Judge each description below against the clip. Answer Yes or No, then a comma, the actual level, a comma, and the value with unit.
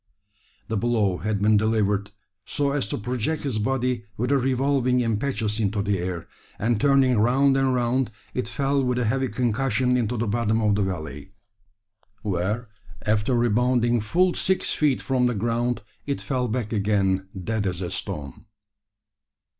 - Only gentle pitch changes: No, average, 3.6 semitones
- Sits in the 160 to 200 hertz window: No, low, 120 Hz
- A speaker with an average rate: Yes, average, 160 wpm